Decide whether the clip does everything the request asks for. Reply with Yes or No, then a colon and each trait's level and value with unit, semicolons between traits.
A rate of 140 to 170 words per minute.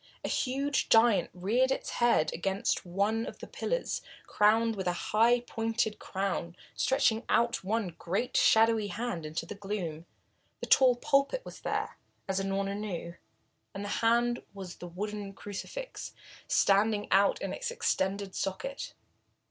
Yes: average, 145 wpm